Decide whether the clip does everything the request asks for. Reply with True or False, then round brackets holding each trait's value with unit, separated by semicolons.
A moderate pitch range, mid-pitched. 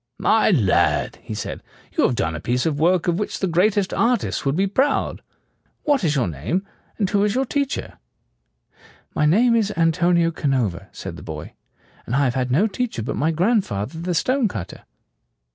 False (8.3 semitones; 170 Hz)